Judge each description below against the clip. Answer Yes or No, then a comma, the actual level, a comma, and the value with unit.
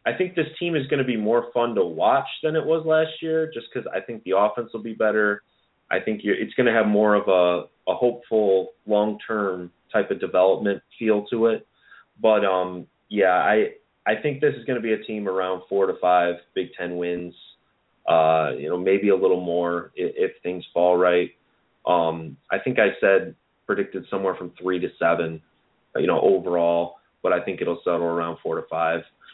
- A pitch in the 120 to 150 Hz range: No, low, 100 Hz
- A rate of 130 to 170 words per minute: No, fast, 205 wpm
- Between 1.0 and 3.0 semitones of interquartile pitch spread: No, average, 5.3 semitones